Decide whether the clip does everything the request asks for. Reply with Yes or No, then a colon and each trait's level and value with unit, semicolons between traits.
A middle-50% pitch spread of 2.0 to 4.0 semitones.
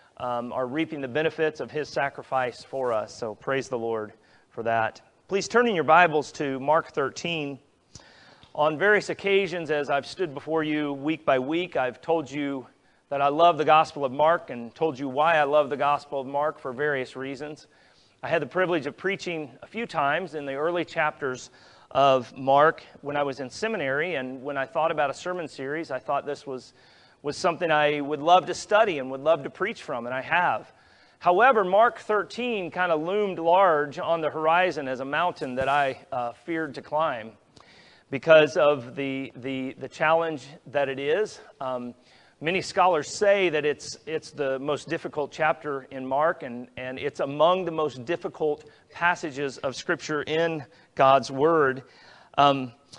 Yes: average, 3.5 semitones